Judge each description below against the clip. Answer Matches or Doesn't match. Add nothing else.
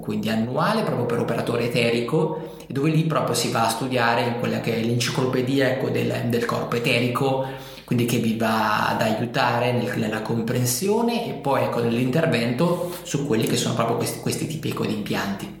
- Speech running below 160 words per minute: Doesn't match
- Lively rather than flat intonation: Doesn't match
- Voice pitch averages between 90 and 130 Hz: Matches